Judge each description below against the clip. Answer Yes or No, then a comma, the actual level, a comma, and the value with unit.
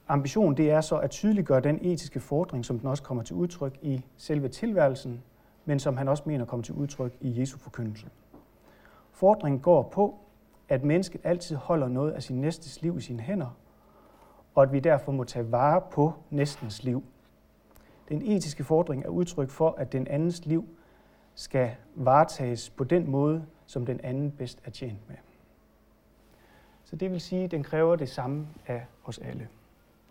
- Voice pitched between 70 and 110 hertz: No, medium, 140 Hz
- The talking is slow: No, average, 175 wpm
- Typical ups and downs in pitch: Yes, average, 3.8 semitones